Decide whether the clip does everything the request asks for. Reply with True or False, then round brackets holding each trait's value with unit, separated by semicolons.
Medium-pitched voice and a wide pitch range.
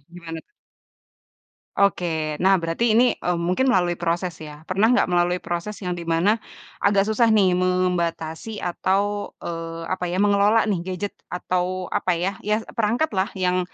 False (180 Hz; 2.9 semitones)